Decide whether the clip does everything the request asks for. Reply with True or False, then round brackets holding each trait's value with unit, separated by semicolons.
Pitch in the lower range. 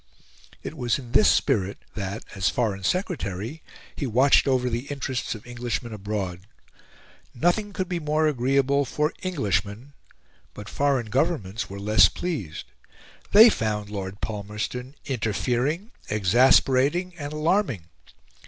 True (125 Hz)